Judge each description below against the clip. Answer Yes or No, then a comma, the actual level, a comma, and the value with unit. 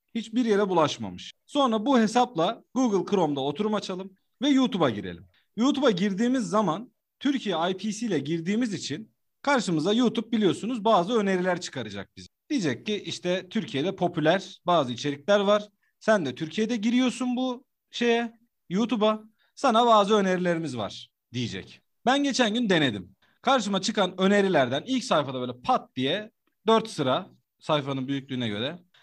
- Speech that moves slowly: No, average, 135 wpm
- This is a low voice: No, high, 200 Hz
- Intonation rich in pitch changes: Yes, wide, 8.1 semitones